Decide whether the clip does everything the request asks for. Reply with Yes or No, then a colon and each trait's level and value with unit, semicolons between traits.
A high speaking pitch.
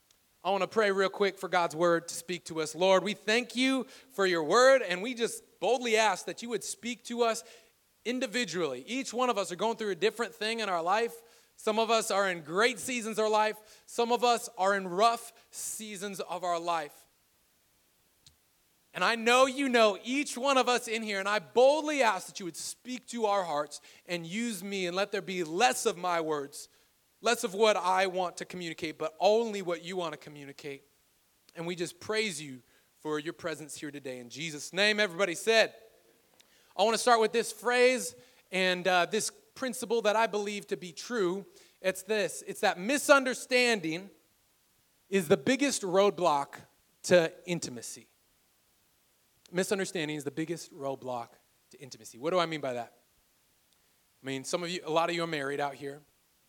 Yes: high, 195 Hz